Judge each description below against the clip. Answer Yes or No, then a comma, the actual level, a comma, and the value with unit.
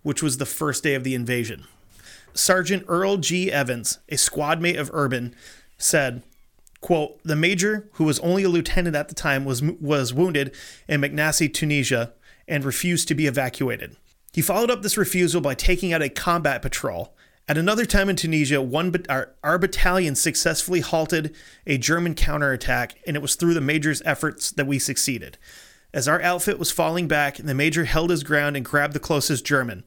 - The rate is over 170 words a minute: Yes, average, 185 wpm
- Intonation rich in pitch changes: No, average, 3.6 semitones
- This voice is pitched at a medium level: Yes, medium, 155 Hz